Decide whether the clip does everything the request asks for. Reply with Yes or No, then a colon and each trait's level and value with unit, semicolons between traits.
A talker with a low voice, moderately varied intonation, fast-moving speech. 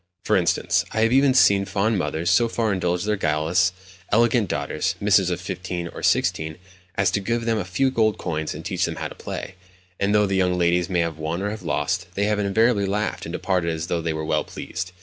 Yes: very low, 95 Hz; average, 3.3 semitones; fast, 220 wpm